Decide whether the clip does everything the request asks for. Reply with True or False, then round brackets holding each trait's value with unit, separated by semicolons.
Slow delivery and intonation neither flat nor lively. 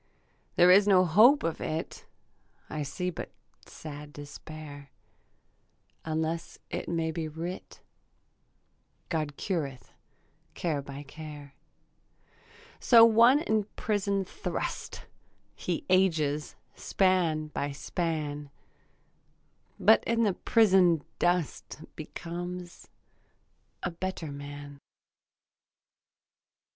True (90 wpm; 3.9 semitones)